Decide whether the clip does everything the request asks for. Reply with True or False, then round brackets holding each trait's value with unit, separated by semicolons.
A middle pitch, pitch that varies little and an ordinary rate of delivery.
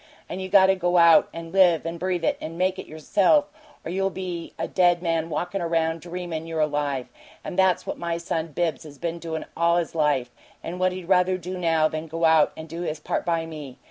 False (170 Hz; 2.1 semitones; 235 wpm)